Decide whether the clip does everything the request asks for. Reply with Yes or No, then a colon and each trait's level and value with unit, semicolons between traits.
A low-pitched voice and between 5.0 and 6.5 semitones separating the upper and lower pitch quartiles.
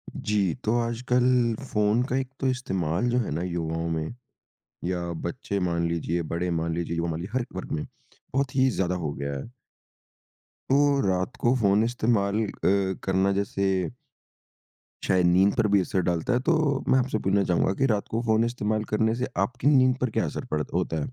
Yes: low, 100 Hz; wide, 5.5 semitones